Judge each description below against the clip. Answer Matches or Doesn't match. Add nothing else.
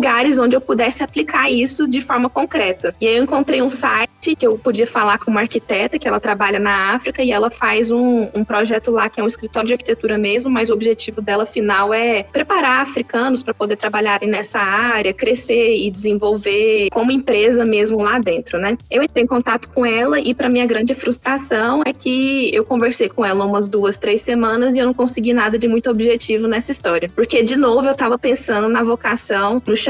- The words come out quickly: Matches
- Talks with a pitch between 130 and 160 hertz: Doesn't match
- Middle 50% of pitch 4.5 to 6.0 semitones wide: Doesn't match